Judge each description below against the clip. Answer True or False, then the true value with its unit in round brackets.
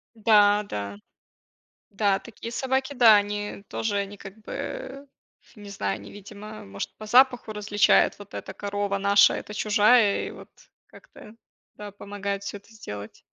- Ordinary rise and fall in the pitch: False (1.5 semitones)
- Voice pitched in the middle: False (205 Hz)